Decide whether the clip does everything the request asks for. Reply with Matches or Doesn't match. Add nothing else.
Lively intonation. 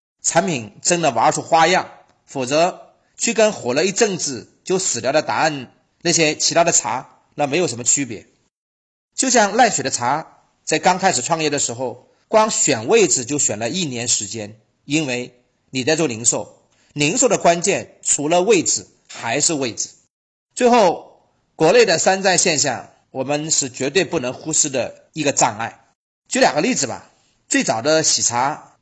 Matches